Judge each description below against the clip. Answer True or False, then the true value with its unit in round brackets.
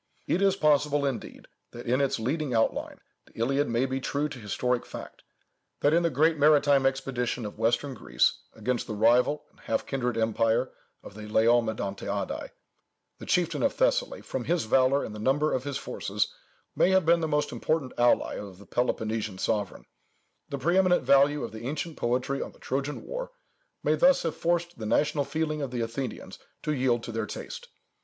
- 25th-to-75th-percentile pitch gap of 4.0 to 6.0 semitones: True (4.7 semitones)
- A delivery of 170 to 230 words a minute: True (185 wpm)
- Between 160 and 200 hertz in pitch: False (135 Hz)